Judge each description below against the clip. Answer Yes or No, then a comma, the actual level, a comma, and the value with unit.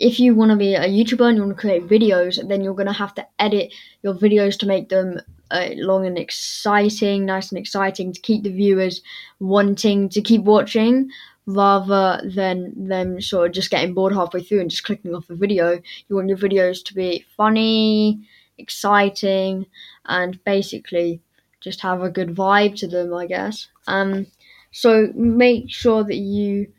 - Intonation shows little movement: Yes, narrow, 1.9 semitones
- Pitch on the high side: Yes, high, 195 Hz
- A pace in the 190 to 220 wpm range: No, average, 180 wpm